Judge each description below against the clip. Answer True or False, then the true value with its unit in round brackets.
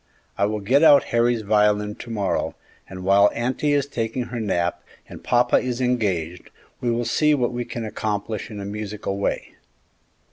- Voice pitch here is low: True (110 Hz)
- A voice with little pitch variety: False (3.2 semitones)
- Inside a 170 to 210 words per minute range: True (175 wpm)